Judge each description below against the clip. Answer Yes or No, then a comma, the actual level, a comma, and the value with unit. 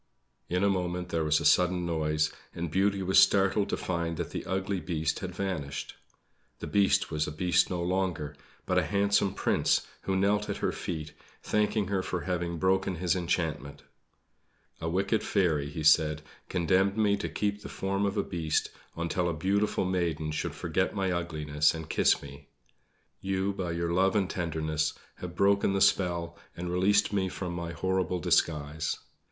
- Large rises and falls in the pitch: No, average, 3.1 semitones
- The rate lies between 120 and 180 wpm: Yes, average, 175 wpm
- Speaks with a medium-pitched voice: No, very low, 90 Hz